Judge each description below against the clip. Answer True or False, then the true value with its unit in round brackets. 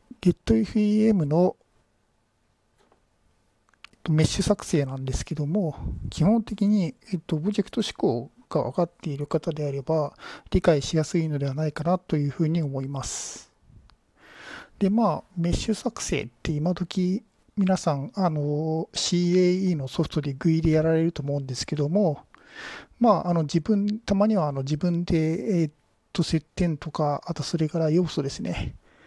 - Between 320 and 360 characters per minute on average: False (275 characters per minute)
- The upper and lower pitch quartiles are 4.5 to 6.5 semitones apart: False (3.8 semitones)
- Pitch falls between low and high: True (165 Hz)